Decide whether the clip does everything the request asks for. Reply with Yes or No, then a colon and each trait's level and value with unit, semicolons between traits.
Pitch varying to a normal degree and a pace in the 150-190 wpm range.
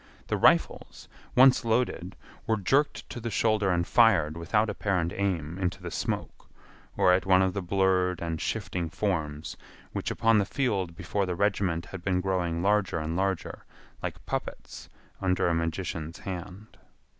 Yes: average, 3.1 semitones; average, 155 wpm